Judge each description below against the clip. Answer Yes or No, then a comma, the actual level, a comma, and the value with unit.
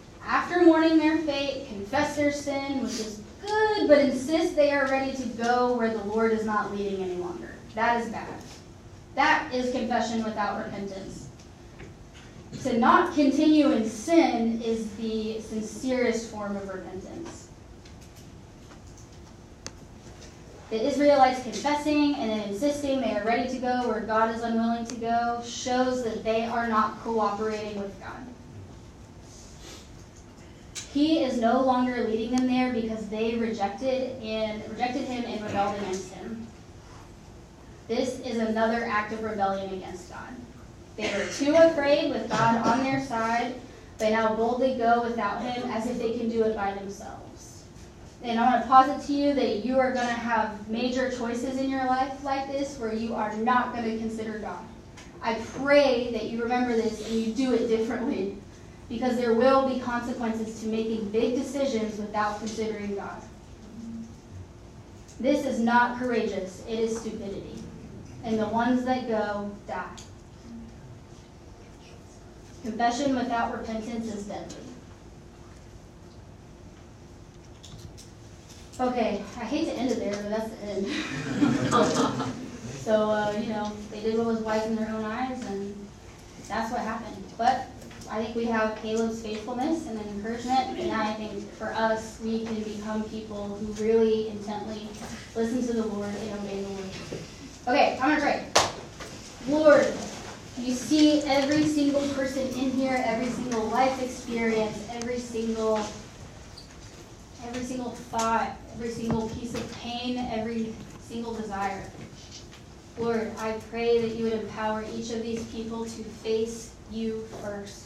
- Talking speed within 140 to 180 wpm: Yes, average, 145 wpm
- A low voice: No, high, 225 Hz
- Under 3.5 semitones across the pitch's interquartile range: Yes, average, 3.1 semitones